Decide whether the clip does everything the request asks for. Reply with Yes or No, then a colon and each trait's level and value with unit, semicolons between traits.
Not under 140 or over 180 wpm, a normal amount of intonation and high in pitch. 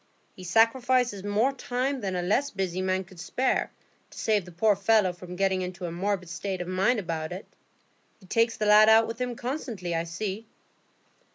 No: average, 190 wpm; average, 4.0 semitones; high, 200 Hz